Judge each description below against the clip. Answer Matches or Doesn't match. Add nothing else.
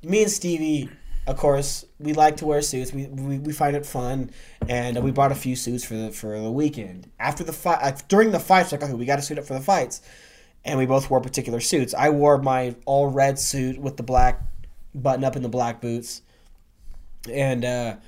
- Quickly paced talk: Matches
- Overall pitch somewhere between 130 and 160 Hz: Matches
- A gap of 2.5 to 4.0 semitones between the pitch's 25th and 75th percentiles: Matches